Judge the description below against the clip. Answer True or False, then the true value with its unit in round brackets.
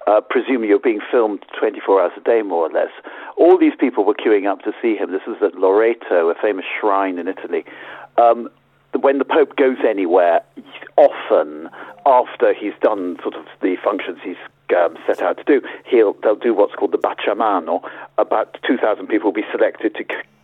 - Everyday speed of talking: True (190 wpm)